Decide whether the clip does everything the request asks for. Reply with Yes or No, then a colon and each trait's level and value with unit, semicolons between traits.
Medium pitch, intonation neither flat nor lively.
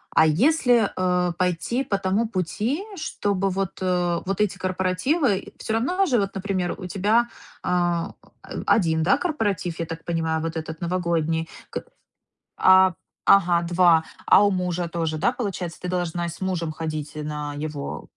Yes: medium, 180 Hz; average, 3.2 semitones